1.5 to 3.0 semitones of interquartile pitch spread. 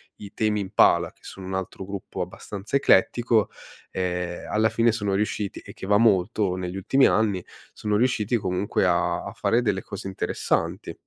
Yes: average, 2.7 semitones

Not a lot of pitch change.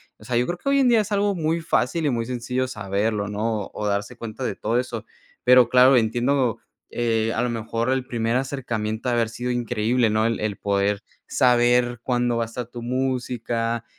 Yes: narrow, 2.2 semitones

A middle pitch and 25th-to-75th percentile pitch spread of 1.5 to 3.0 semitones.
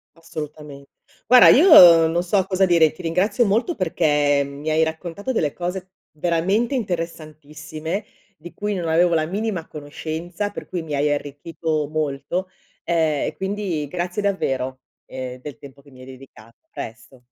No: medium, 160 Hz; average, 4.1 semitones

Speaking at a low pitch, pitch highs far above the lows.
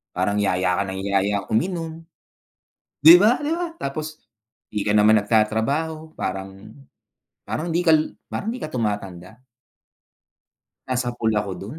Yes: low, 110 Hz; wide, 7.8 semitones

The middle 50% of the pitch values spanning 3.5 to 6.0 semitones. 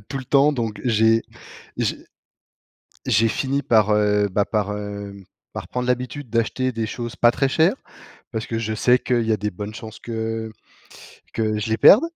No: average, 2.8 semitones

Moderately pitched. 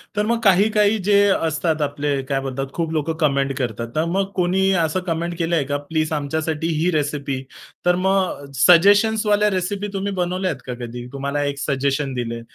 Yes: medium, 160 Hz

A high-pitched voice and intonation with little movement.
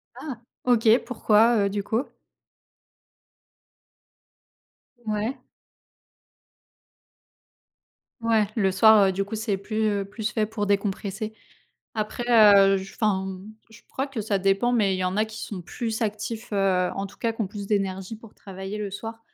Yes: high, 210 Hz; narrow, 2.2 semitones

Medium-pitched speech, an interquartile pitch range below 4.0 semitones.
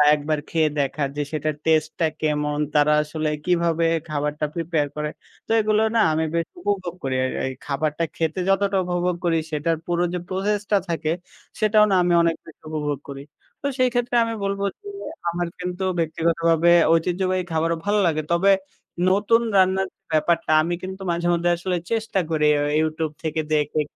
Yes: medium, 165 Hz; average, 3.3 semitones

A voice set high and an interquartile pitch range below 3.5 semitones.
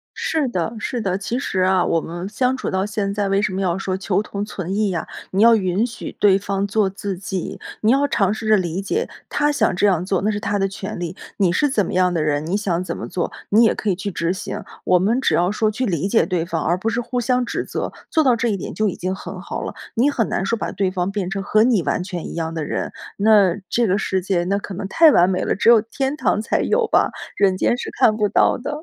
Yes: high, 200 Hz; average, 3.1 semitones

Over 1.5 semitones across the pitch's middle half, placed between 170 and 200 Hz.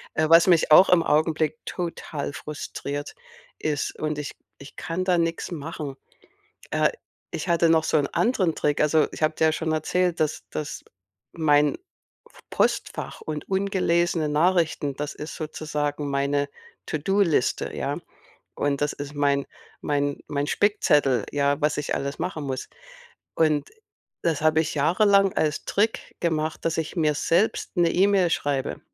No: narrow, 2.6 semitones; medium, 155 Hz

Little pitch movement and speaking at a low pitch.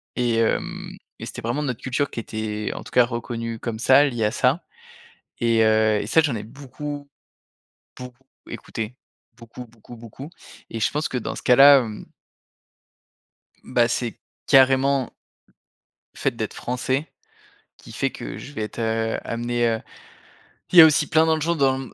No: average, 3.3 semitones; low, 120 Hz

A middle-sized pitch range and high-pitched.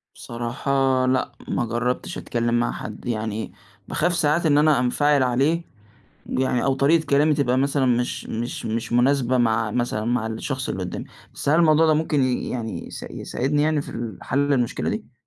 No: average, 3.6 semitones; low, 130 Hz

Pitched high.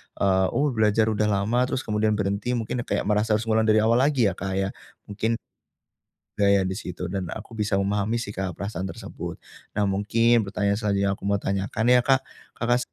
No: low, 105 Hz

